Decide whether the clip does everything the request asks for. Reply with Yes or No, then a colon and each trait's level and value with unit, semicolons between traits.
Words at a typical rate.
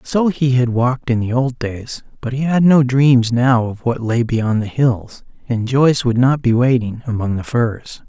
No: fast, 215 wpm